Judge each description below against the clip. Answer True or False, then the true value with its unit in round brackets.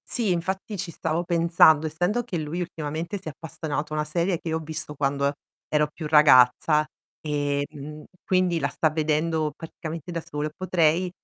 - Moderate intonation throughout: False (2.3 semitones)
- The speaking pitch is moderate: True (160 Hz)